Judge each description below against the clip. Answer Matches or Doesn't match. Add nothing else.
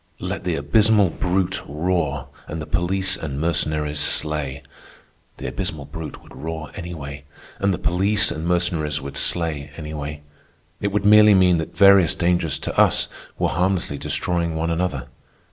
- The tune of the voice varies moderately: Matches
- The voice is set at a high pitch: Doesn't match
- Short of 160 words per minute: Matches